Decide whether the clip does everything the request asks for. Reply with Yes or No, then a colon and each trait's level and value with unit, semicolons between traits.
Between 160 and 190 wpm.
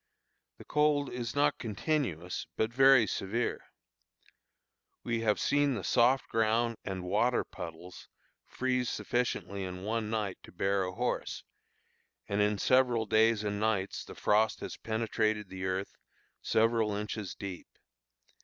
No: slow, 135 wpm